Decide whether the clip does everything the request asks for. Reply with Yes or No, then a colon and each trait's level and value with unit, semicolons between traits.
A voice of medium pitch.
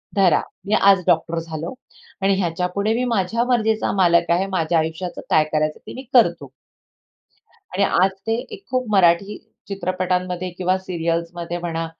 Yes: medium, 180 Hz